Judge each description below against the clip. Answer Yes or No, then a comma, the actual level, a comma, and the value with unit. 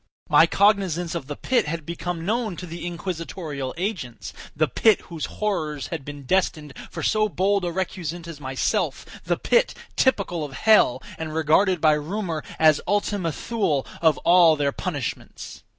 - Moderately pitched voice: Yes, medium, 170 Hz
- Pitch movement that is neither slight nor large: Yes, average, 4.2 semitones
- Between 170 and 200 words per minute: No, average, 155 wpm